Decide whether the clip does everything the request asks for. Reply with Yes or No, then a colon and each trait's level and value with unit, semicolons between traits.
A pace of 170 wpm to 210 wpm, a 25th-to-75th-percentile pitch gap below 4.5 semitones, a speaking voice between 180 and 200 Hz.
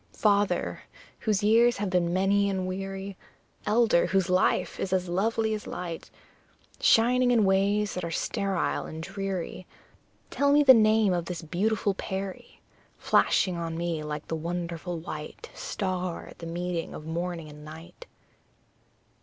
No: average, 145 wpm; average, 3.2 semitones; medium, 185 Hz